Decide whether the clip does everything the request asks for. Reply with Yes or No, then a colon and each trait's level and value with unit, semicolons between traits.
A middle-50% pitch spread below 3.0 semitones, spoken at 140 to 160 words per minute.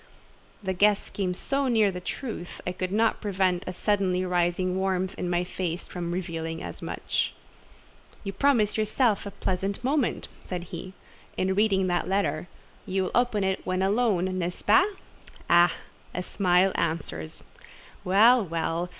Yes: narrow, 2.5 semitones; average, 150 wpm